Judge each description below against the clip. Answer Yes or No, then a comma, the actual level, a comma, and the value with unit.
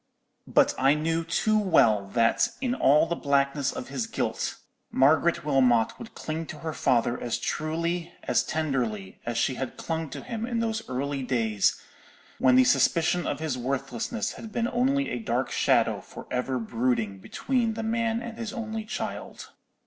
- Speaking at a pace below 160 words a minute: No, average, 170 wpm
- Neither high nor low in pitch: Yes, medium, 155 Hz